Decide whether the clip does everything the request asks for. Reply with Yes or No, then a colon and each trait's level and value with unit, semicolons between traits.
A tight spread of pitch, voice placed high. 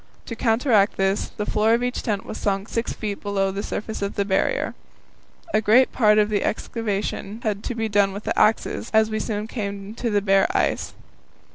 Yes: narrow, 1.8 semitones; high, 210 Hz